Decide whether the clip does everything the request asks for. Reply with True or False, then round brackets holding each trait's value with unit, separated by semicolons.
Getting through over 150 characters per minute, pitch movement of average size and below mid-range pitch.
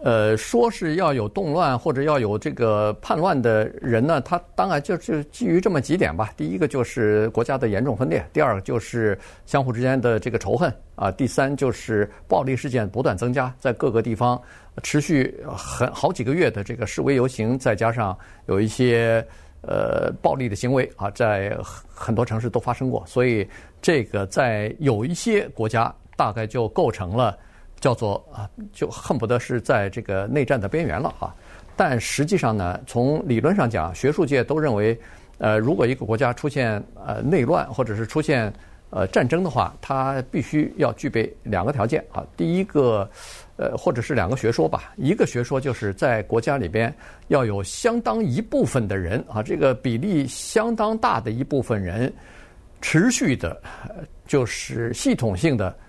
True (265 characters per minute; 4.4 semitones; 120 Hz)